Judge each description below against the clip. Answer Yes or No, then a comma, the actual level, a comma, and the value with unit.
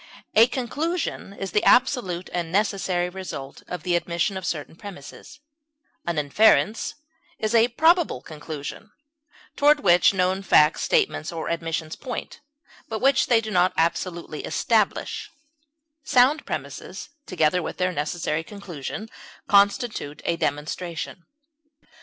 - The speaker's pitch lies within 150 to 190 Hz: Yes, medium, 185 Hz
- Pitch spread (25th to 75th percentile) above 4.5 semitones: Yes, average, 5.2 semitones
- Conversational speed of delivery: No, slow, 125 wpm